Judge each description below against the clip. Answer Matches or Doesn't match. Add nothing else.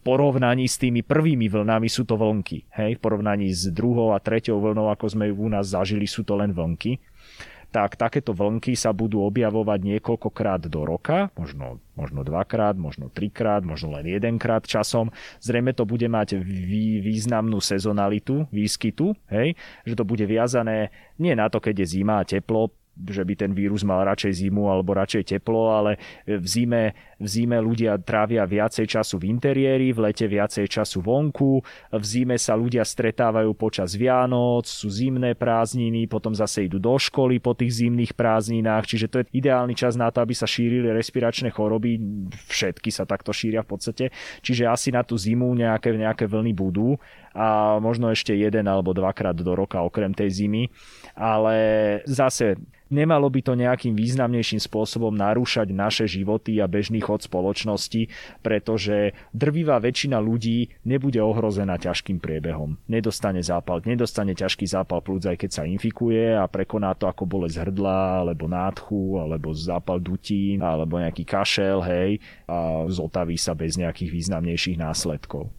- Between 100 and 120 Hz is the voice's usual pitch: Matches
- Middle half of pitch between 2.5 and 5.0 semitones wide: Matches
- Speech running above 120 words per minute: Matches